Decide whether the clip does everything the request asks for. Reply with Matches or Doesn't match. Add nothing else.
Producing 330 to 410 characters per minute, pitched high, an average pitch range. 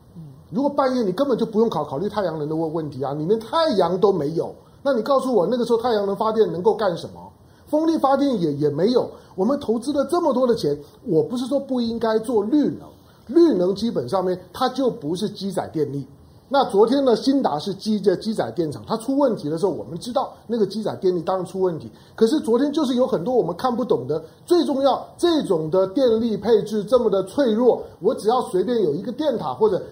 Doesn't match